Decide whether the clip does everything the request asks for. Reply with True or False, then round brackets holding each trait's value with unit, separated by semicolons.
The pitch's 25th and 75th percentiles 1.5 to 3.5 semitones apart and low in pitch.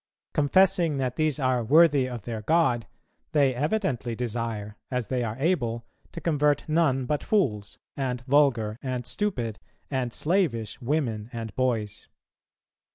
False (4.4 semitones; 130 Hz)